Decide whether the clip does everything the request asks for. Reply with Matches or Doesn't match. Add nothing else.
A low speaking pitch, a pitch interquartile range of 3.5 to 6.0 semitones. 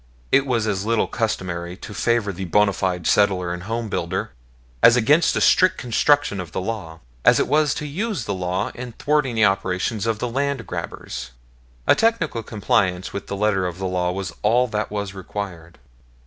Matches